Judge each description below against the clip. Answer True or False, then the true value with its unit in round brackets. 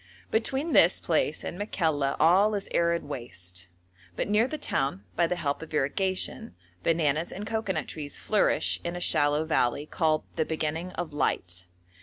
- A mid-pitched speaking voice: True (160 Hz)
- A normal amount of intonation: True (4.6 semitones)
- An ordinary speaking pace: True (160 wpm)